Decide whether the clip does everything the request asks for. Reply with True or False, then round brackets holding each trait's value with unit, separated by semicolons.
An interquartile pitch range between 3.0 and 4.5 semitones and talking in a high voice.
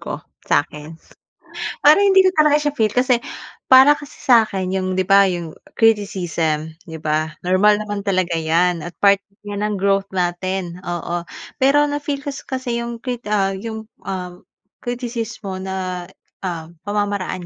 False (5.0 semitones; 195 Hz)